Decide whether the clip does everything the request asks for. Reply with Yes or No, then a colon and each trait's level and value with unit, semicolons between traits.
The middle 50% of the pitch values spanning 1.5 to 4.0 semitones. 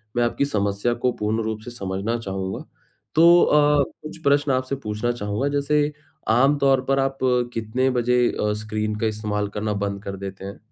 No: average, 4.6 semitones